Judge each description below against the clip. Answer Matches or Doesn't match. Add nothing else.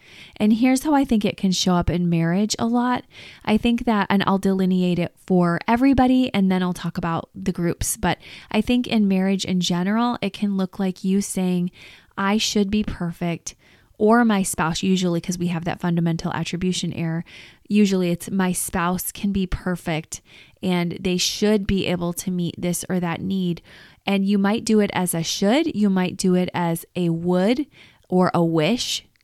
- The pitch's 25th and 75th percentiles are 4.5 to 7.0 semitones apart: Doesn't match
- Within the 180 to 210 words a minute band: Matches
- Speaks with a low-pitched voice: Doesn't match